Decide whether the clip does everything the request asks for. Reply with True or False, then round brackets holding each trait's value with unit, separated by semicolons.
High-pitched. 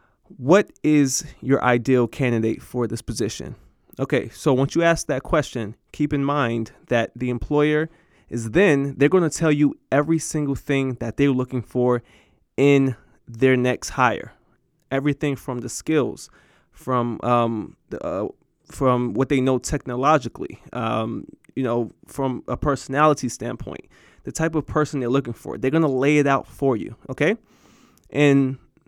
False (135 Hz)